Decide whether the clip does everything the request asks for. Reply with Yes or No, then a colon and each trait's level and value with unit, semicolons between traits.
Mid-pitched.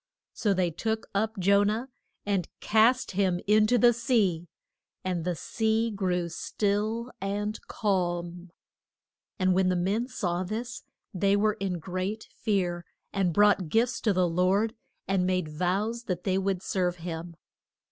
No: high, 195 Hz